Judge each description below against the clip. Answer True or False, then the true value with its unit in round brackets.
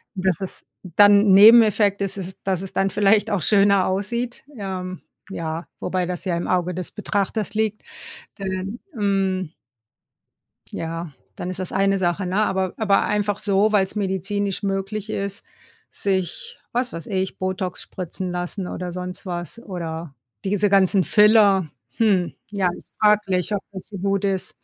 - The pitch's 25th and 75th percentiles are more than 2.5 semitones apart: False (2.0 semitones)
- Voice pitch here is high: True (195 Hz)